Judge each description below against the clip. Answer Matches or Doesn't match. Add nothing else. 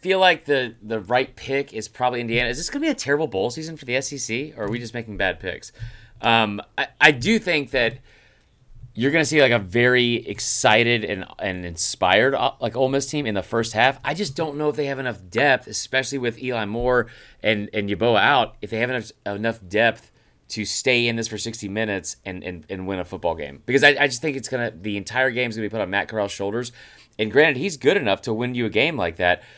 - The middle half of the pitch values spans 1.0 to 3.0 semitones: Doesn't match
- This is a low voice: Matches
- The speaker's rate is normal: Doesn't match